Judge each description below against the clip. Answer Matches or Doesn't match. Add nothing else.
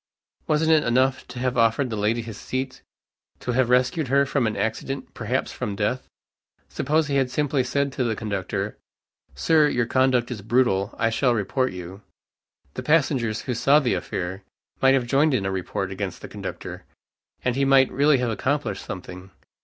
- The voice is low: Matches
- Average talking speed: Matches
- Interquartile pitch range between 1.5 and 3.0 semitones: Doesn't match